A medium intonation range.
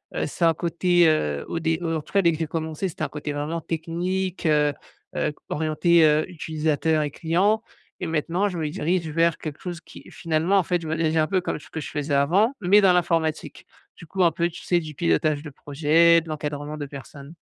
No: narrow, 2.3 semitones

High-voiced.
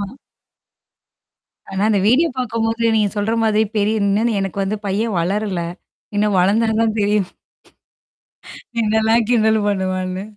Yes: high, 210 Hz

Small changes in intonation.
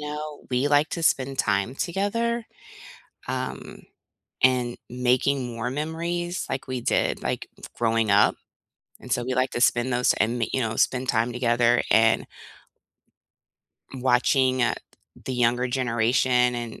Yes: narrow, 2.3 semitones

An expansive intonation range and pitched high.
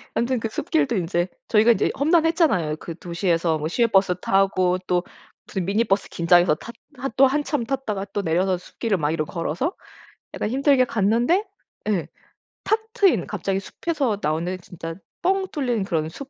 Yes: wide, 7.0 semitones; high, 195 Hz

